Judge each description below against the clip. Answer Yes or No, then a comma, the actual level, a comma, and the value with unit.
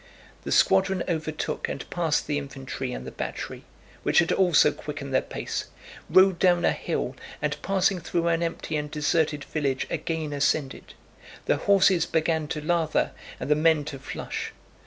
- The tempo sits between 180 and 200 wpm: No, average, 155 wpm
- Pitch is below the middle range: No, medium, 155 Hz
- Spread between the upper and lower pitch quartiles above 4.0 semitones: No, average, 2.8 semitones